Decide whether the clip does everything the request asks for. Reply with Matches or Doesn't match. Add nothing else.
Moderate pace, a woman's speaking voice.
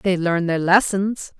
Matches